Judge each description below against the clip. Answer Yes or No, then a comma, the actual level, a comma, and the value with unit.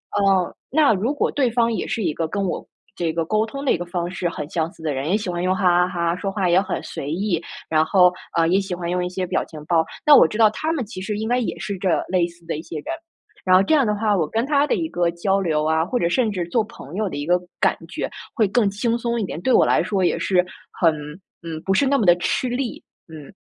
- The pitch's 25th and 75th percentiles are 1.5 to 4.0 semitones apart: No, average, 4.4 semitones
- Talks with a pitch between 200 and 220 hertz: No, medium, 185 Hz